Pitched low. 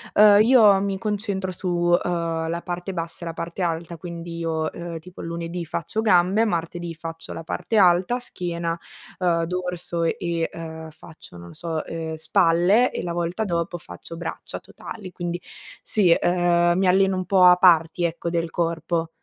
No: medium, 175 Hz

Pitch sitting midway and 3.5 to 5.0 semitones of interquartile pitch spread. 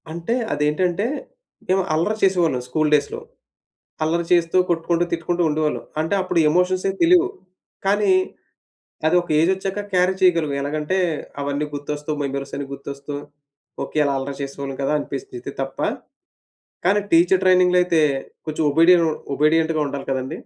Yes: medium, 165 Hz; average, 3.8 semitones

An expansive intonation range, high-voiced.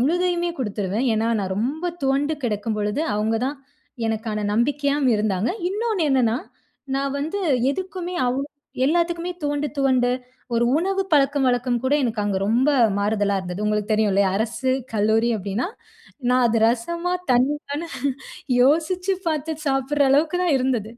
Yes: wide, 5.8 semitones; very high, 260 Hz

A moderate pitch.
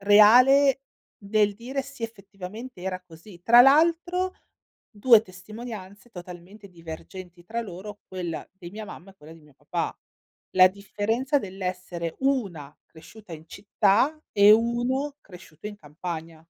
No: high, 200 Hz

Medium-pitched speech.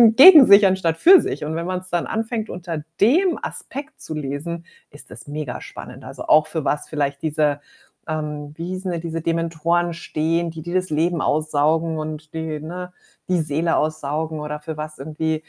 Yes: medium, 160 Hz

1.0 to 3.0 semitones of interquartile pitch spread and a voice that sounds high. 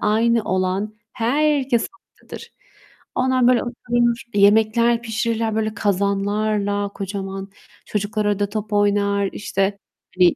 Yes: narrow, 2.5 semitones; high, 215 Hz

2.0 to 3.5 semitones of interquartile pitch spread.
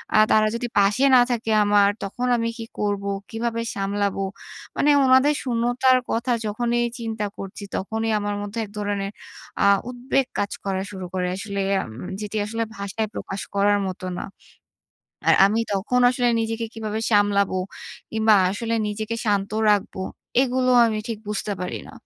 Yes: narrow, 2.5 semitones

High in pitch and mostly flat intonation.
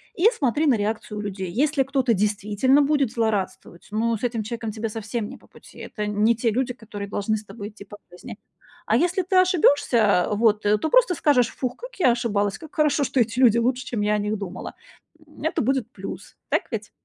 No: high, 230 Hz; average, 4.4 semitones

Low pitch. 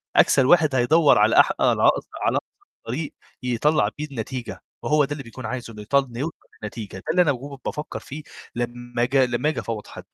Yes: low, 130 Hz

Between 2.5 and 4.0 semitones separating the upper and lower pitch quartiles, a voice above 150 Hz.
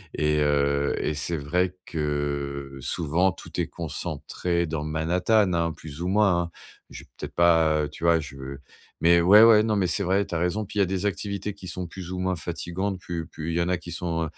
No: average, 3.0 semitones; very low, 85 Hz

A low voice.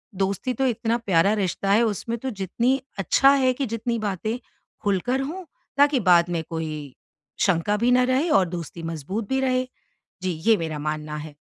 No: high, 215 Hz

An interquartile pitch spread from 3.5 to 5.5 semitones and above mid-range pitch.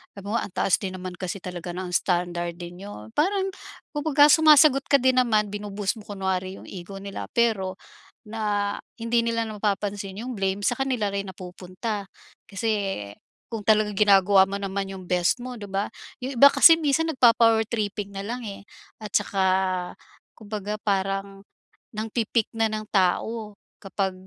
No: average, 3.1 semitones; high, 205 Hz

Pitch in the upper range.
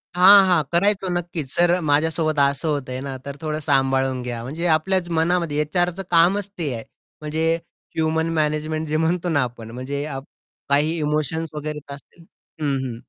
No: medium, 155 Hz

